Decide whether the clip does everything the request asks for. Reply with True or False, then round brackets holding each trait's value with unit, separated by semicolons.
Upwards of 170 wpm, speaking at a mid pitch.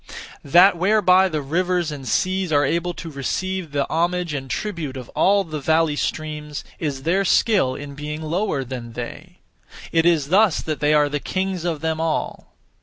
True (180 wpm; 160 Hz)